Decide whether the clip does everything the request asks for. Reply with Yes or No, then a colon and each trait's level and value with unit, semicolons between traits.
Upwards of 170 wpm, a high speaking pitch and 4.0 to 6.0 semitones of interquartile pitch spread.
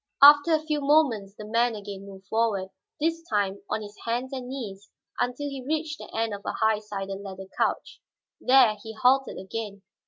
Yes: average, 185 wpm; high, 225 Hz; average, 5.0 semitones